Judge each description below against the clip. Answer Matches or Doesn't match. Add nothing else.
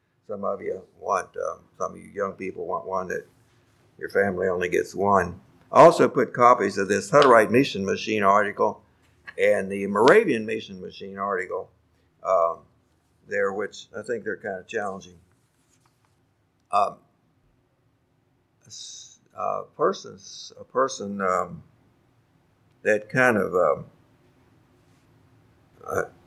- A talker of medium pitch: Doesn't match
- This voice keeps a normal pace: Doesn't match